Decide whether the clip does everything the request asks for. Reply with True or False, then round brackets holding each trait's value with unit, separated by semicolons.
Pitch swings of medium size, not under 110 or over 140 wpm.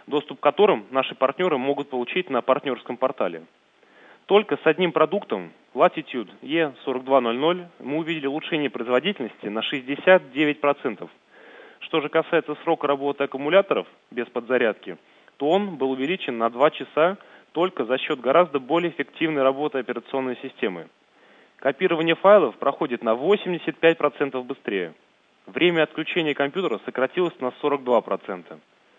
True (4.0 semitones; 120 wpm)